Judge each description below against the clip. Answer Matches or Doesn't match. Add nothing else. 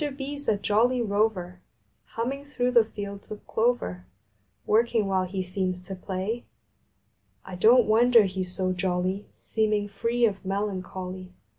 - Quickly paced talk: Doesn't match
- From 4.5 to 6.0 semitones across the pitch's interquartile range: Doesn't match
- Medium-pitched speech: Doesn't match